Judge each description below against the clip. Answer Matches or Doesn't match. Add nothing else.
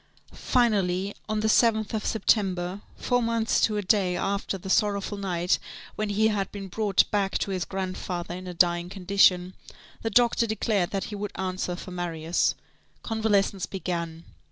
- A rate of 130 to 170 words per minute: Matches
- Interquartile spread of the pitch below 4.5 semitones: Matches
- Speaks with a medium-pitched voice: Doesn't match